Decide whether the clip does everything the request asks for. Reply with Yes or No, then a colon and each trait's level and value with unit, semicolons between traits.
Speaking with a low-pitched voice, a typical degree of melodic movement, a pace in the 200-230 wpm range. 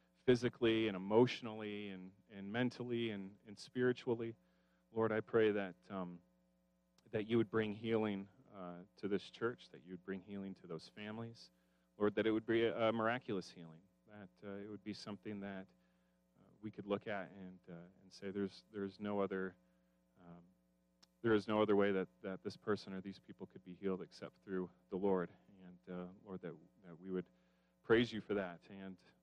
No: low, 100 Hz; average, 3.3 semitones; average, 190 wpm